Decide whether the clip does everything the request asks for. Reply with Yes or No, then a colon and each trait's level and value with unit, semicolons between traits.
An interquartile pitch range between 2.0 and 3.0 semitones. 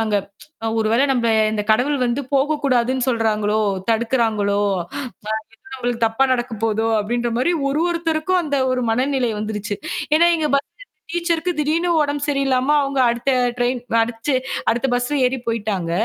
No: average, 4.1 semitones